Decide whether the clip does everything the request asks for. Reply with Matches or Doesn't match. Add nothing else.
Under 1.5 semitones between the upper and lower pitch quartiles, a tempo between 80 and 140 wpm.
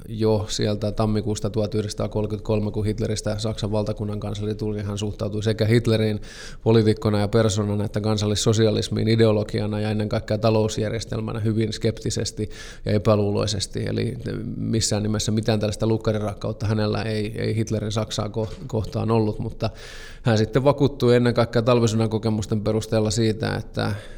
Matches